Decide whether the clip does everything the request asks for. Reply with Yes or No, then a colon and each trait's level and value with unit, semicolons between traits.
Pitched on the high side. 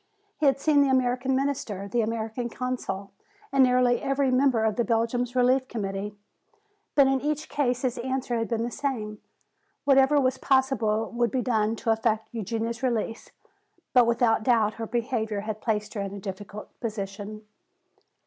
Yes: high, 235 Hz